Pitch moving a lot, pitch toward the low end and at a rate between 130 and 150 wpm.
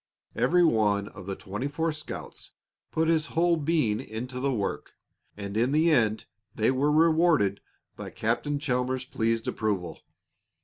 Yes: wide, 6.4 semitones; low, 125 Hz; average, 145 wpm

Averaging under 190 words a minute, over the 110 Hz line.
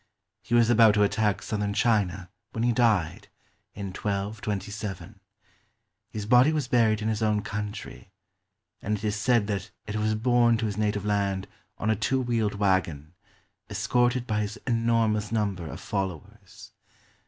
No: average, 155 wpm; low, 105 Hz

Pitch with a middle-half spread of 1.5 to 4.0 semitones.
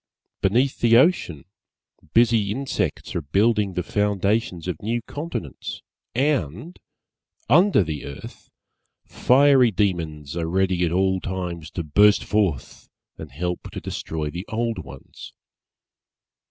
No: wide, 5.6 semitones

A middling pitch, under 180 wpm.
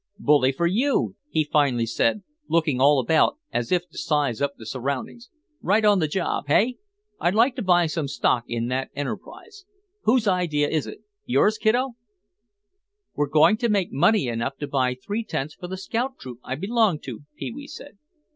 No: medium, 165 Hz; average, 185 wpm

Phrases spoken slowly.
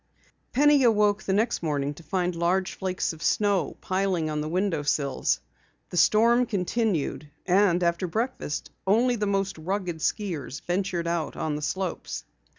No: average, 155 wpm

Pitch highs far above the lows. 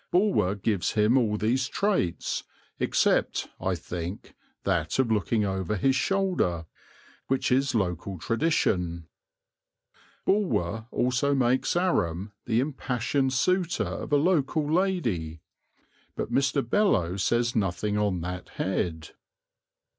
Yes: wide, 7.3 semitones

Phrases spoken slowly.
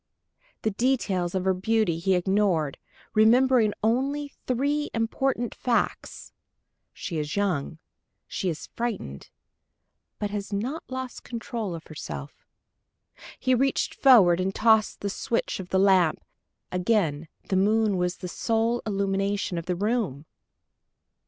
Yes: slow, 125 wpm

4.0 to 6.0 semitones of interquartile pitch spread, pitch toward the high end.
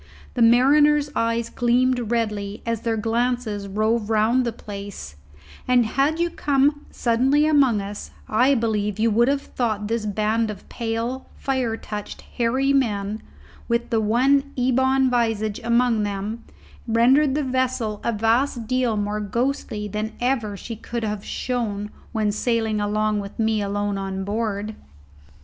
No: average, 3.2 semitones; high, 230 Hz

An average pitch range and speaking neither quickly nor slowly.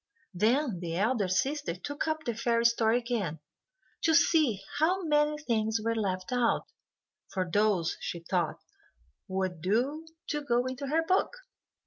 No: wide, 7.5 semitones; average, 145 wpm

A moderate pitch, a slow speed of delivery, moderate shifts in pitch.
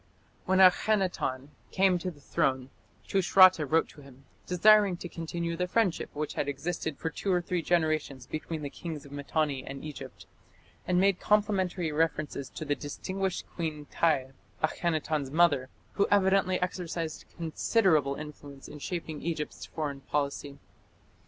No: medium, 160 Hz; average, 145 wpm; average, 3.8 semitones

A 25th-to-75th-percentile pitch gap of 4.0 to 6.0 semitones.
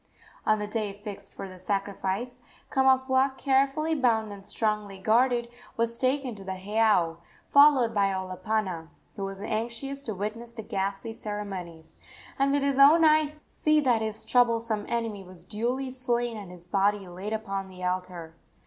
Yes: average, 4.6 semitones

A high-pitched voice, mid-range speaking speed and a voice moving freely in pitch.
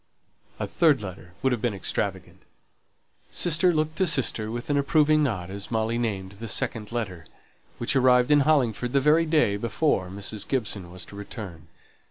No: low, 120 Hz; average, 170 wpm; wide, 6.4 semitones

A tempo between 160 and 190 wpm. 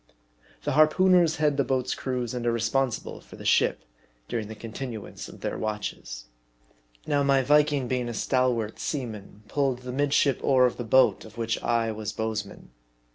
Yes: average, 170 wpm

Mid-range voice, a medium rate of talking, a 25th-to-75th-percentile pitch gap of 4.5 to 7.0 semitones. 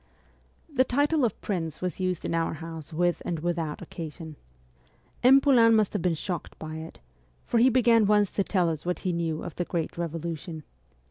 Yes: medium, 175 Hz; average, 190 wpm; average, 4.9 semitones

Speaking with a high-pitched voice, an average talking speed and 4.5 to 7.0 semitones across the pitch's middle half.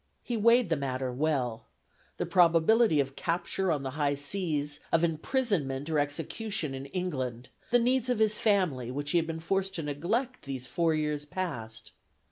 No: medium, 160 Hz; average, 170 wpm; wide, 5.6 semitones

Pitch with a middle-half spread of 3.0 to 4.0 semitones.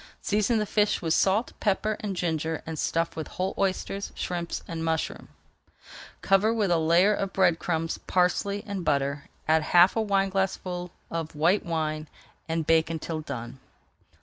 Yes: average, 3.5 semitones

